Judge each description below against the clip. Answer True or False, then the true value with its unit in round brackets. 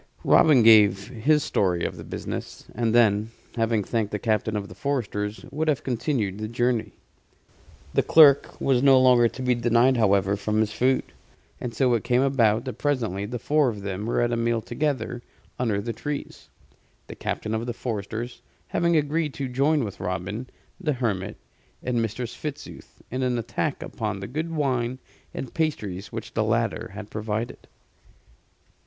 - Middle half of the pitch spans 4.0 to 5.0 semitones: False (3.5 semitones)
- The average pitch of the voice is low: True (120 Hz)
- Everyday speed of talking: True (170 wpm)